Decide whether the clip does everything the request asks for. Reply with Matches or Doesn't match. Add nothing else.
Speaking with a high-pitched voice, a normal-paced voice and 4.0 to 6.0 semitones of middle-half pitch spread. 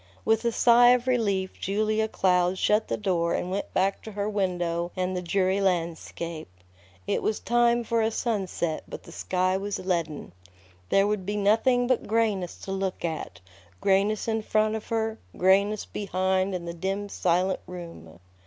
Doesn't match